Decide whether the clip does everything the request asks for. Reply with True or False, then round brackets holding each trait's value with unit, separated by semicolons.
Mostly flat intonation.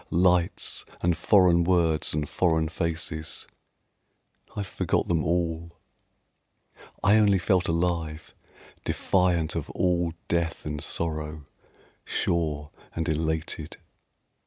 True (1.9 semitones)